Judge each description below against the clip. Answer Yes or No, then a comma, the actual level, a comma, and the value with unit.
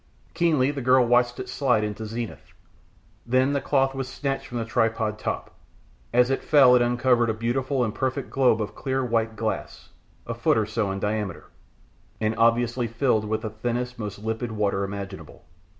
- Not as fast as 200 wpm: Yes, average, 180 wpm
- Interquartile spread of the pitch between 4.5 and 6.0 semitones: No, average, 2.9 semitones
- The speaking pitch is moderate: No, low, 120 Hz